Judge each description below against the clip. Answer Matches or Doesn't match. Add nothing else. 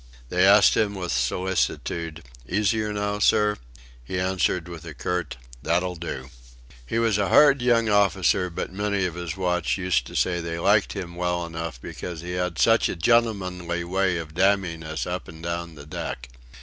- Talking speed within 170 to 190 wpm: Matches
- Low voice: Matches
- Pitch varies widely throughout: Doesn't match